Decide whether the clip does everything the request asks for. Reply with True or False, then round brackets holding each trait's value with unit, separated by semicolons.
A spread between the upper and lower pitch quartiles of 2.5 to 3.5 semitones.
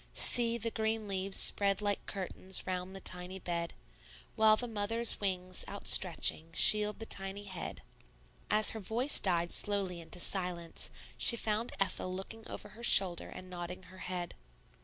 True (3.0 semitones)